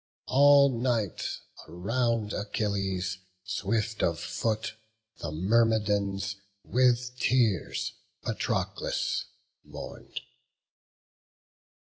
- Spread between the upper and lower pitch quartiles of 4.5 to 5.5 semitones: No, average, 3.5 semitones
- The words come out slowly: Yes, slow, 65 wpm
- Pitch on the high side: No, low, 110 Hz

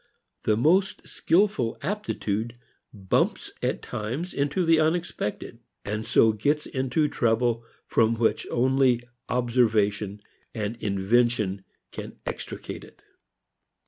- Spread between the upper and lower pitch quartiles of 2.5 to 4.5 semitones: No, average, 5.0 semitones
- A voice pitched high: No, low, 120 Hz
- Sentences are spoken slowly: Yes, slow, 100 wpm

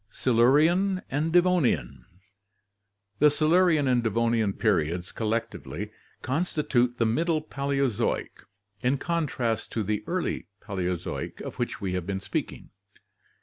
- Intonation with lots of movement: Yes, wide, 7.1 semitones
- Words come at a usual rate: No, slow, 115 wpm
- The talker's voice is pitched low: Yes, low, 120 Hz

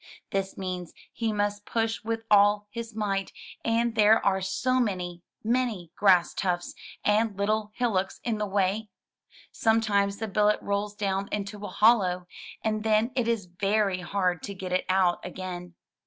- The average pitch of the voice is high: Yes, high, 205 Hz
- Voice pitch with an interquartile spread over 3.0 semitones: No, narrow, 2.6 semitones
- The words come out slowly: No, average, 160 wpm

